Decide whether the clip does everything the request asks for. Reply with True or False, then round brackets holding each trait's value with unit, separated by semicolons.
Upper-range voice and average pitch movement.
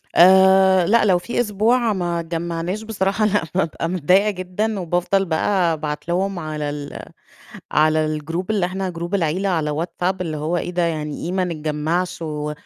False (175 Hz; 3.2 semitones)